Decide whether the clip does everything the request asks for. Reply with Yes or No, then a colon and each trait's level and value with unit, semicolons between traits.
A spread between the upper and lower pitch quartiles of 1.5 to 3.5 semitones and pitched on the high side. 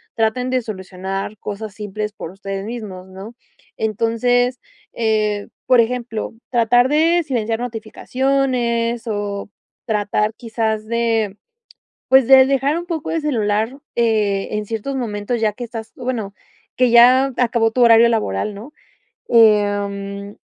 Yes: average, 2.9 semitones; high, 225 Hz